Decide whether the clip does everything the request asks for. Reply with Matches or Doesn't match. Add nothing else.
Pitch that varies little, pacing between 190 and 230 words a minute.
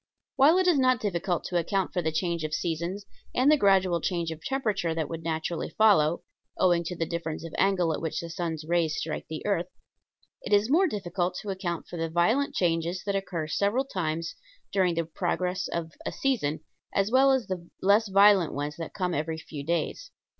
Doesn't match